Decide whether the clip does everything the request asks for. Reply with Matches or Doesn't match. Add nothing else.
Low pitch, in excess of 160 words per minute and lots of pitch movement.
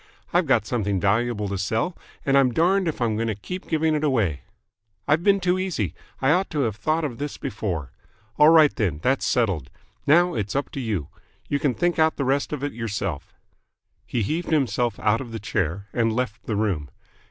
Matches